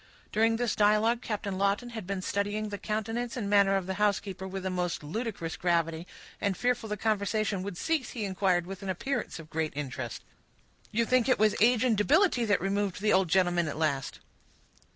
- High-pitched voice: Yes, high, 200 Hz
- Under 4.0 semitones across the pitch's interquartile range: Yes, average, 3.3 semitones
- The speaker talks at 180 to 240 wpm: Yes, average, 195 wpm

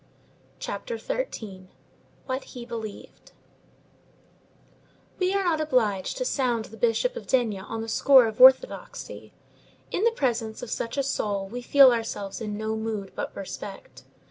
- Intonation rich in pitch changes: No, average, 4.3 semitones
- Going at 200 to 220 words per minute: No, average, 145 wpm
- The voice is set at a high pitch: Yes, high, 235 Hz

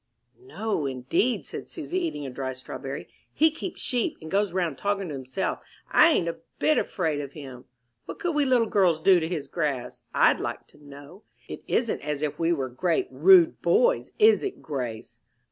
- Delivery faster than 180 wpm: Yes, average, 190 wpm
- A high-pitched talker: No, medium, 170 Hz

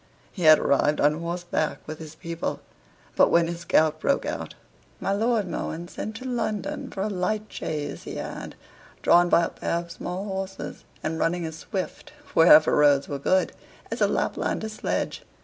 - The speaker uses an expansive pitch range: No, average, 4.1 semitones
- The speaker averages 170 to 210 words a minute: Yes, average, 175 wpm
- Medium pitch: Yes, medium, 170 Hz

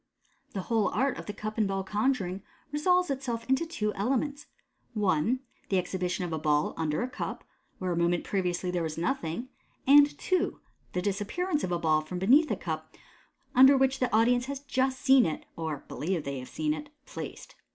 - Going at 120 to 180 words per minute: No, average, 195 wpm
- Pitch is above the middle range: Yes, high, 210 Hz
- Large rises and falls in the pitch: Yes, wide, 7.3 semitones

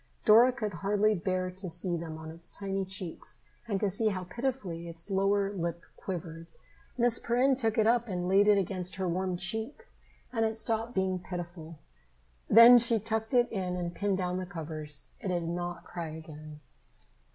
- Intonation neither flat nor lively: Yes, average, 4.2 semitones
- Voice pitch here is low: No, high, 190 Hz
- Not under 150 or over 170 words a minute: No, average, 180 wpm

